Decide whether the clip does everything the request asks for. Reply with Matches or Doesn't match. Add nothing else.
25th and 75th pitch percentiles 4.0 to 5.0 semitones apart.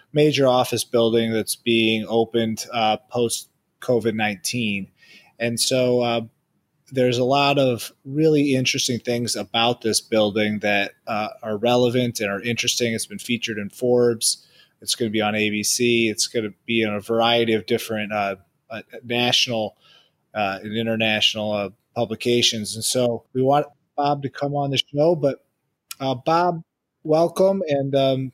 Doesn't match